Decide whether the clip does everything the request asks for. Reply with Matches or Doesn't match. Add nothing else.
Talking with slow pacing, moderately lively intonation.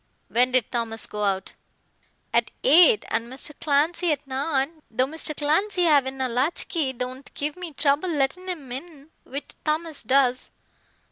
Doesn't match